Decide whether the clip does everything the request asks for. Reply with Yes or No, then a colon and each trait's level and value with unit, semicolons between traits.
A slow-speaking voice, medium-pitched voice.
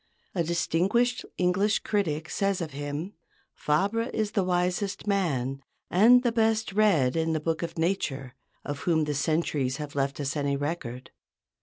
No: average, 155 wpm; medium, 170 Hz